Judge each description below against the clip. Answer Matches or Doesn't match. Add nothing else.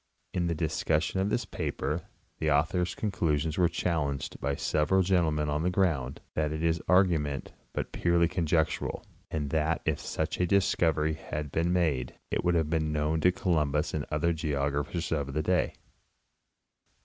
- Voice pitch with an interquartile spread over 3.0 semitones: Doesn't match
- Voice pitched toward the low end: Matches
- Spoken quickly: Doesn't match